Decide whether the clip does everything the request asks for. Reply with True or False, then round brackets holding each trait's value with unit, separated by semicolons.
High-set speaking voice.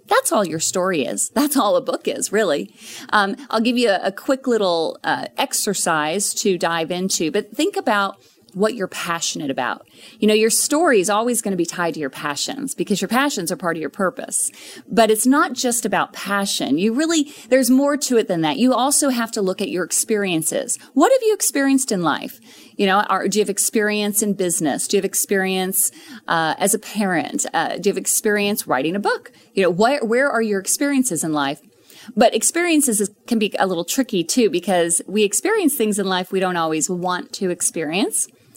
True (210 Hz)